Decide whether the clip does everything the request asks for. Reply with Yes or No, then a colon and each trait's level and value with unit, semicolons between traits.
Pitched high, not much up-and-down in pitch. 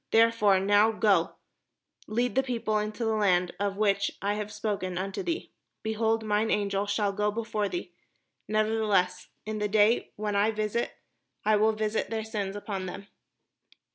Yes: high, 210 Hz; narrow, 1.6 semitones